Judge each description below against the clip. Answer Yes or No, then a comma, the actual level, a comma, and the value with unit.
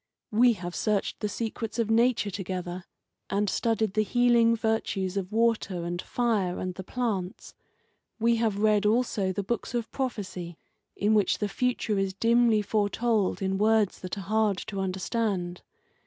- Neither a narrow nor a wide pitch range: Yes, average, 3.2 semitones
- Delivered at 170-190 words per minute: No, average, 155 wpm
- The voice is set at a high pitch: Yes, high, 210 Hz